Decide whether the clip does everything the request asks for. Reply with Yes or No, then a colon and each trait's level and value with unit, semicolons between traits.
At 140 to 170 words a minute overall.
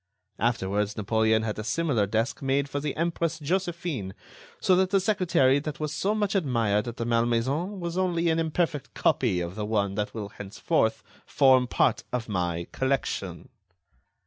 Yes: average, 165 wpm